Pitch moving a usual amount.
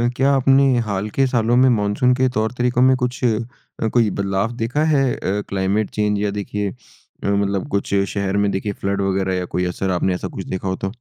Yes: average, 4.0 semitones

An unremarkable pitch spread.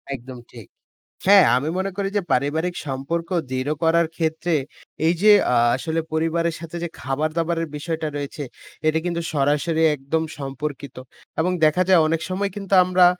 Yes: average, 3.1 semitones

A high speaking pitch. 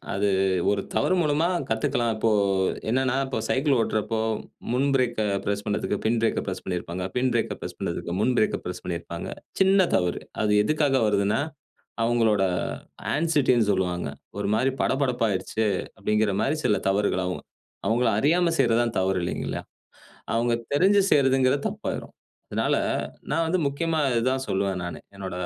No: low, 115 Hz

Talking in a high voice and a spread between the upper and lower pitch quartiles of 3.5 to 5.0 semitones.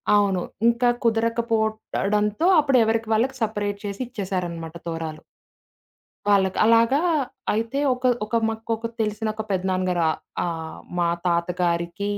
Yes: high, 210 Hz; average, 4.0 semitones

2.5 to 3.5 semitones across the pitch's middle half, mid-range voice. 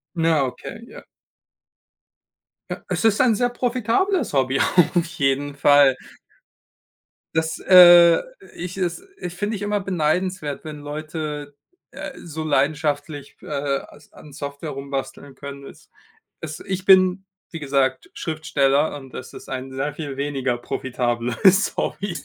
No: average, 4.5 semitones; medium, 150 Hz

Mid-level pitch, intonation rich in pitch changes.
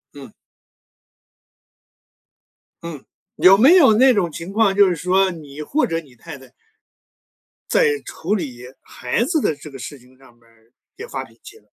Yes: medium, 165 Hz; wide, 8.0 semitones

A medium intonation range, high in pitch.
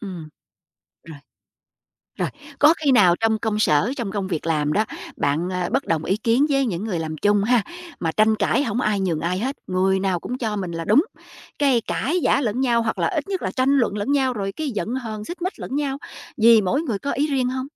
No: wide, 5.8 semitones; high, 220 Hz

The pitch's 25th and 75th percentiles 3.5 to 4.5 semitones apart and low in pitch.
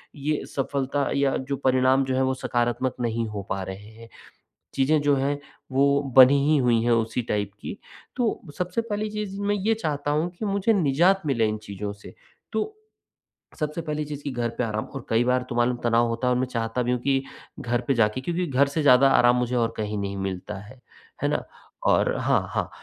Yes: average, 4.2 semitones; low, 130 Hz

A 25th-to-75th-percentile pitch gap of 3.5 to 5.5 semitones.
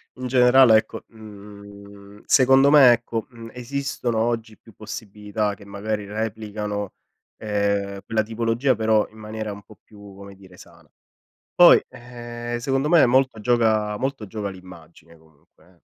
No: average, 2.8 semitones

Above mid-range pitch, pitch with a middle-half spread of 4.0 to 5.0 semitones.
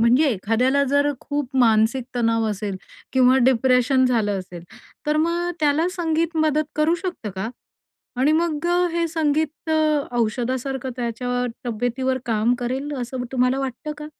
Yes: very high, 260 Hz; average, 4.5 semitones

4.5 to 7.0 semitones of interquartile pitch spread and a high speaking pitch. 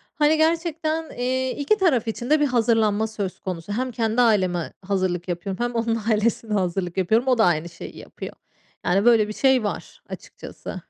Yes: average, 5.1 semitones; high, 225 Hz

